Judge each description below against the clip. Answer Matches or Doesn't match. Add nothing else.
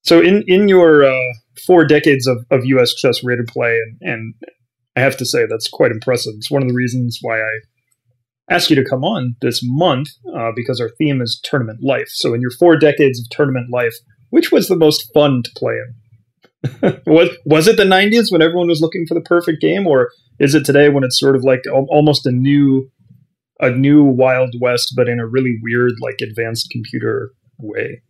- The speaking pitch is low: Matches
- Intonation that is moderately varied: Matches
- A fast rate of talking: Matches